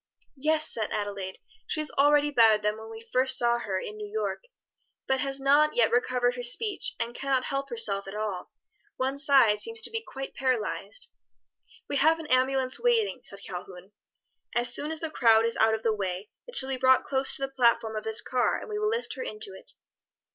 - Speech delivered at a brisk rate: Yes, fast, 210 wpm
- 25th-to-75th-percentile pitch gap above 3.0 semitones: Yes, average, 5.1 semitones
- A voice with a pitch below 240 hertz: No, very high, 260 Hz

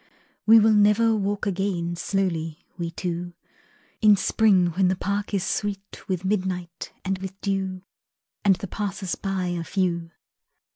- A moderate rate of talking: Yes, average, 145 wpm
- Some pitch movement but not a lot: No, narrow, 2.3 semitones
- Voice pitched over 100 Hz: Yes, high, 190 Hz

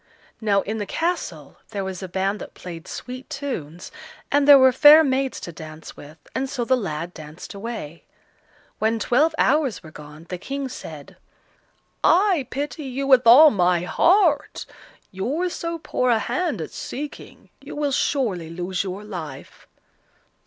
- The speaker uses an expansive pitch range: Yes, wide, 8.0 semitones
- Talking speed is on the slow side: No, average, 160 wpm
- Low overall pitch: No, high, 230 Hz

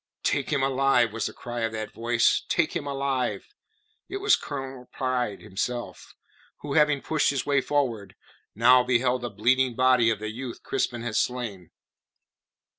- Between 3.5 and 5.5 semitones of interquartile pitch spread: No, average, 2.8 semitones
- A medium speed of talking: Yes, average, 160 wpm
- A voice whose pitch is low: Yes, low, 125 Hz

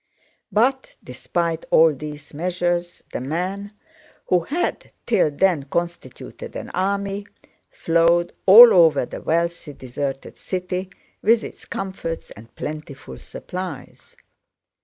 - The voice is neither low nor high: Yes, medium, 175 Hz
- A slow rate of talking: Yes, slow, 110 wpm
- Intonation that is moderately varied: Yes, average, 3.8 semitones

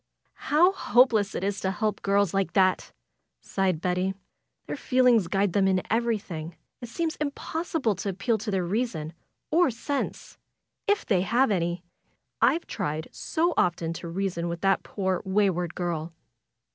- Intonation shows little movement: No, average, 5.0 semitones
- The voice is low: No, high, 195 Hz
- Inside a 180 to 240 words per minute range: No, average, 150 wpm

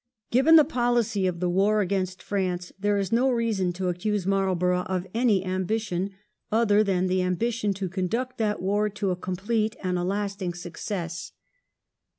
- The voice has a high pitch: Yes, high, 195 Hz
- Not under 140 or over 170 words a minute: Yes, average, 165 wpm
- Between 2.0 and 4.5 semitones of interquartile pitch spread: Yes, average, 2.9 semitones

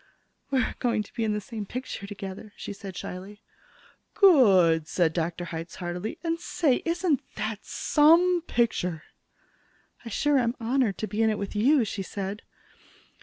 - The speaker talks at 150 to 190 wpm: Yes, average, 160 wpm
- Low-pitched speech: No, high, 215 Hz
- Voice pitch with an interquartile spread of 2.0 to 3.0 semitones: No, wide, 5.4 semitones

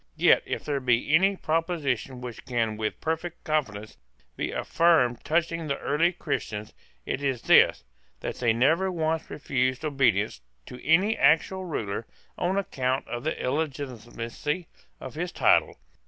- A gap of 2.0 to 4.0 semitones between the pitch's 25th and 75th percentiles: No, average, 5.2 semitones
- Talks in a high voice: No, medium, 140 Hz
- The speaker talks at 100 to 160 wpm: Yes, average, 140 wpm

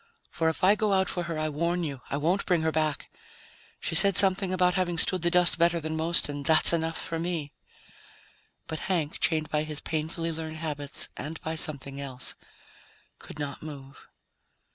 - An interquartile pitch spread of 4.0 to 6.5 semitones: No, narrow, 2.4 semitones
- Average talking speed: Yes, average, 185 wpm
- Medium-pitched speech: Yes, medium, 160 Hz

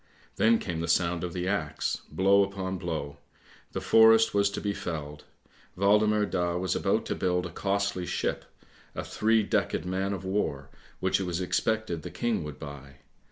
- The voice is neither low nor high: No, very low, 95 Hz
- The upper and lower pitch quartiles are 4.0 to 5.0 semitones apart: No, average, 3.1 semitones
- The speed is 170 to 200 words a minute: Yes, average, 175 wpm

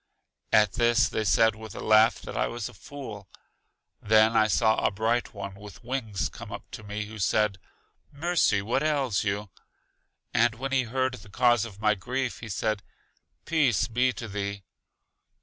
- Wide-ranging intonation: No, average, 3.0 semitones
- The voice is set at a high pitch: No, low, 110 Hz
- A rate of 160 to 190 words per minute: Yes, average, 175 wpm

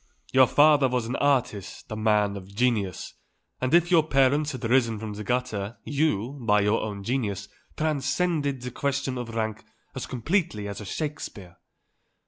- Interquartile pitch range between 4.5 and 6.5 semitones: Yes, average, 5.0 semitones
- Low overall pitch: Yes, low, 125 Hz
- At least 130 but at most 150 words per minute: No, average, 160 wpm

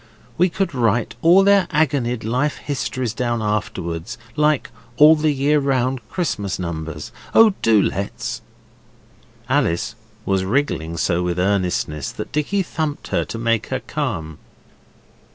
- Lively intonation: Yes, wide, 7.8 semitones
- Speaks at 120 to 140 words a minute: Yes, slow, 135 wpm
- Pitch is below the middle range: Yes, low, 120 Hz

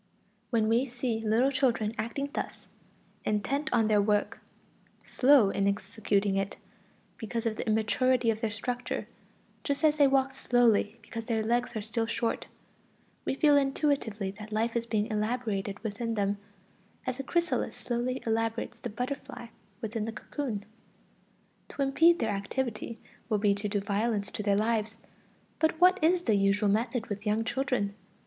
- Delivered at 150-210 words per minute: Yes, average, 155 wpm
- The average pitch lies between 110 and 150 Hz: No, high, 225 Hz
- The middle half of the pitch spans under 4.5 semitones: Yes, average, 3.4 semitones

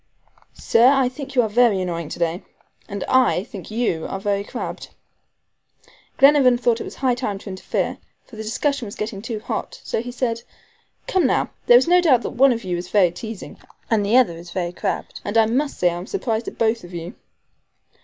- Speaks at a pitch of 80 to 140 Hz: No, high, 225 Hz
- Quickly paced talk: Yes, fast, 210 wpm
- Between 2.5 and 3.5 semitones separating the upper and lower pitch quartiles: No, average, 4.6 semitones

